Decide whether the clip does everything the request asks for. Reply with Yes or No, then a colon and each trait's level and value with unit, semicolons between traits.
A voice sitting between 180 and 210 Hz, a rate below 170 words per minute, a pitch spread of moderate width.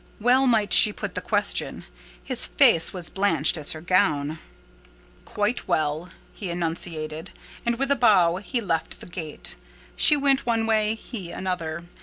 No: high, 190 Hz; average, 155 wpm; wide, 5.7 semitones